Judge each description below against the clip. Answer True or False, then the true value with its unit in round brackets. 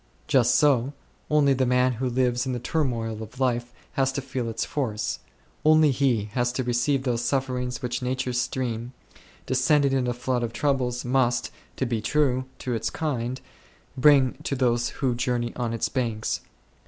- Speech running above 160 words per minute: True (170 wpm)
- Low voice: True (125 Hz)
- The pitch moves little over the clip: True (1.9 semitones)